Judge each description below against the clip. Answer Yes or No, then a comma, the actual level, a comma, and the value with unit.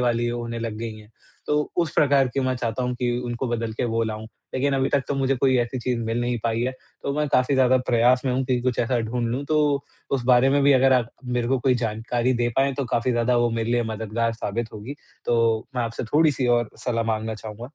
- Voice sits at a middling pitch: No, low, 120 Hz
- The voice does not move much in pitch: Yes, narrow, 2.1 semitones